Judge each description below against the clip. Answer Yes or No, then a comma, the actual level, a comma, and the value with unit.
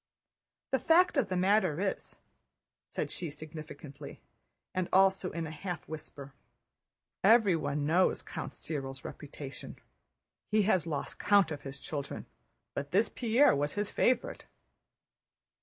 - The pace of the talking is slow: Yes, slow, 125 wpm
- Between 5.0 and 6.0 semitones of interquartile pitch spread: Yes, wide, 5.5 semitones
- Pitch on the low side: No, medium, 170 Hz